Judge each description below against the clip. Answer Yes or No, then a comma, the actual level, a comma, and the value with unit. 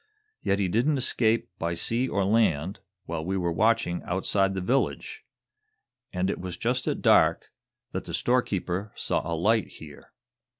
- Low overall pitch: Yes, very low, 95 Hz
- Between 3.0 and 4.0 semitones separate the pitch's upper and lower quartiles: No, average, 4.7 semitones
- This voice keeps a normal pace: Yes, average, 160 wpm